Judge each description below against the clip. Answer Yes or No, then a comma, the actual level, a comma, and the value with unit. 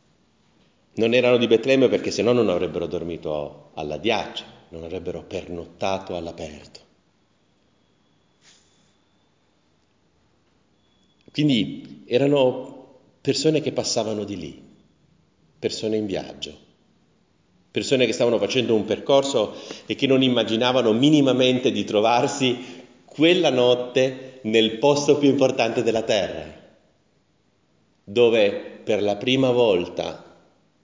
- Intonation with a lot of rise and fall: No, average, 4.0 semitones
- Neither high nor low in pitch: No, low, 120 Hz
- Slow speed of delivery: Yes, slow, 100 wpm